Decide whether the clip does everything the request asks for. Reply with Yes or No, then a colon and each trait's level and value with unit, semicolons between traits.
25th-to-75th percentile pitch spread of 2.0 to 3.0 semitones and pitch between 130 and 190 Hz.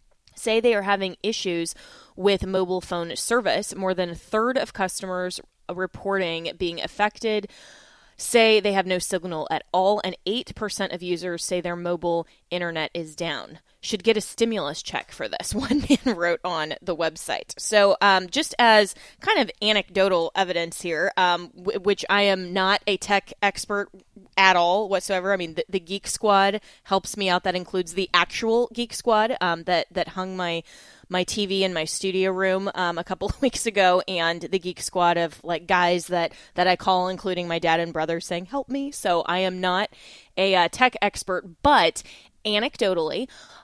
Yes: average, 2.7 semitones; medium, 185 Hz